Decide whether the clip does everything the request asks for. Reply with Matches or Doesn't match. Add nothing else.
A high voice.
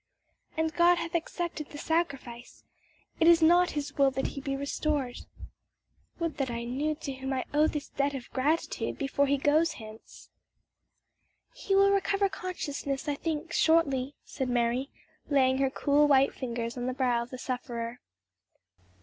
Matches